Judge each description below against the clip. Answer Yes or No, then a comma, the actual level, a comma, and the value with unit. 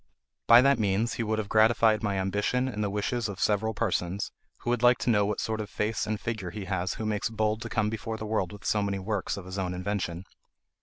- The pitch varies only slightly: Yes, narrow, 2.0 semitones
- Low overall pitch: Yes, low, 105 Hz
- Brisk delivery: Yes, fast, 245 wpm